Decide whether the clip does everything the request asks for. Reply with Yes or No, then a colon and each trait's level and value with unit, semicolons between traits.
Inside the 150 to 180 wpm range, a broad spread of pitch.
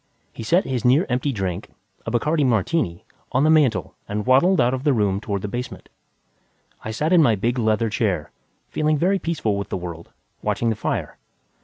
No: average, 190 wpm; wide, 6.2 semitones